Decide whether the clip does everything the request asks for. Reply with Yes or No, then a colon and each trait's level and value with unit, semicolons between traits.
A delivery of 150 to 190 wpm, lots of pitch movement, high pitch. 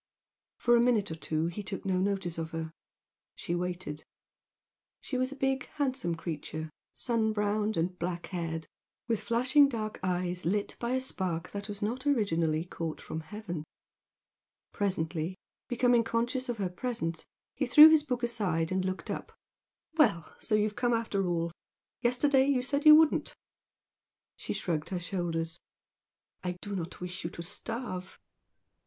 Yes: average, 155 wpm; wide, 5.9 semitones; high, 200 Hz